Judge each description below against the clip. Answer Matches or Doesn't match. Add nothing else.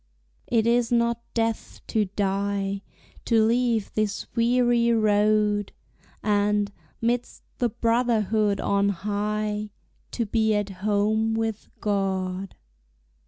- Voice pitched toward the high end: Matches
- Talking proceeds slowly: Matches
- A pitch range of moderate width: Doesn't match